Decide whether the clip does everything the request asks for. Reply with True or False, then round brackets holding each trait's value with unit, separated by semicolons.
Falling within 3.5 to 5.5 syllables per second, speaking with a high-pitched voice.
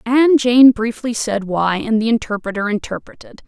True (4.8 syllables/s; 225 Hz)